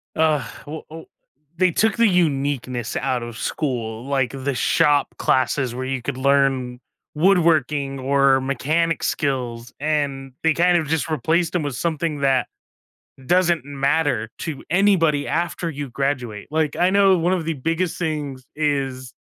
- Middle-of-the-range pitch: Yes, medium, 145 Hz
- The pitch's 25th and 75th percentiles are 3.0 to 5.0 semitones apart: Yes, average, 3.7 semitones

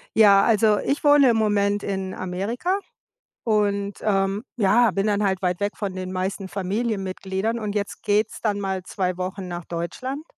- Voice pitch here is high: Yes, high, 200 Hz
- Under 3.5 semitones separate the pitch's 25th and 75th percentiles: Yes, narrow, 2.4 semitones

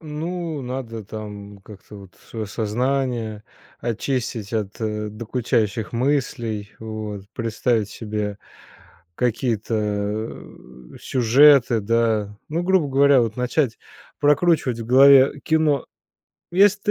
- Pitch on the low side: Yes, low, 115 Hz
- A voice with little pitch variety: No, average, 4.4 semitones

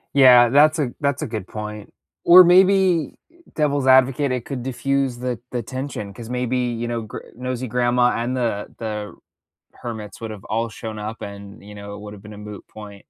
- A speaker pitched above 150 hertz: No, low, 120 Hz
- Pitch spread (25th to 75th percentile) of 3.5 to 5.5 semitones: Yes, average, 3.8 semitones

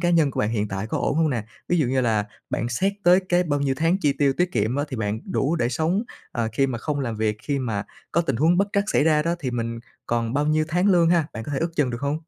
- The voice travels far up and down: Yes, wide, 5.9 semitones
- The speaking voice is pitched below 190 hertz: Yes, medium, 140 Hz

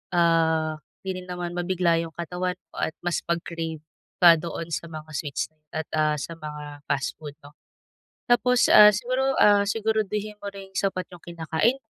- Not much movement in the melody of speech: No, average, 4.0 semitones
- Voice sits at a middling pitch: Yes, medium, 170 Hz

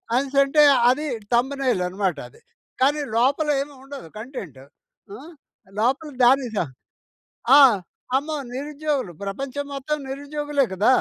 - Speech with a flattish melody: No, average, 3.3 semitones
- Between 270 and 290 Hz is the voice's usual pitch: Yes, very high, 275 Hz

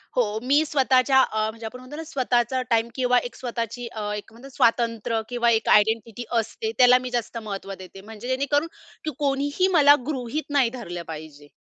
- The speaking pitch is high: Yes, high, 240 Hz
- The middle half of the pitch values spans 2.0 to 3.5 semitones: Yes, average, 3.2 semitones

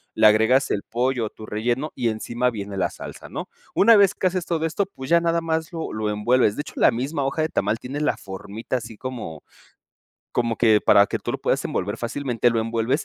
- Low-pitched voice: Yes, low, 120 Hz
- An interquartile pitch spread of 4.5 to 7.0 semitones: Yes, wide, 5.5 semitones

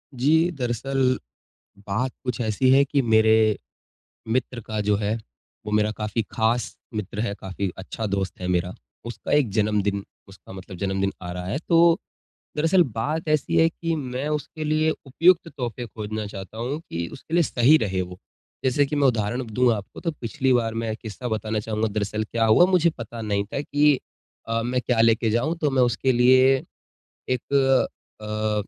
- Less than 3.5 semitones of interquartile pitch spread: No, average, 4.2 semitones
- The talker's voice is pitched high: No, low, 115 Hz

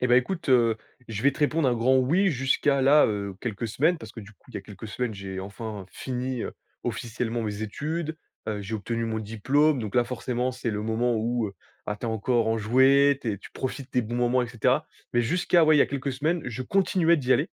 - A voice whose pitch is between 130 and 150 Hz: No, low, 120 Hz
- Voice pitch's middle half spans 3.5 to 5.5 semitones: Yes, average, 3.9 semitones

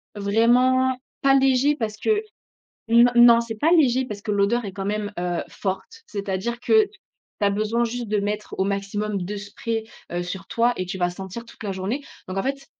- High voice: Yes, high, 215 Hz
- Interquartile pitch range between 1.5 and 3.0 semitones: No, average, 3.7 semitones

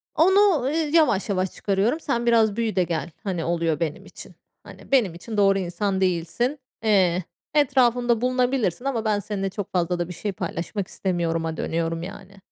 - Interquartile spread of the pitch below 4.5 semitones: No, wide, 5.6 semitones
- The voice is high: Yes, high, 200 Hz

